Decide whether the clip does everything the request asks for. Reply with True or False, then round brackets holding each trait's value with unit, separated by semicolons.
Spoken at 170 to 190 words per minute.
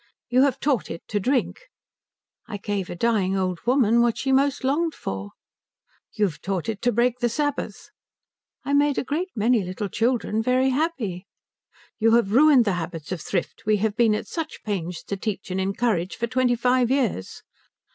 True (180 wpm)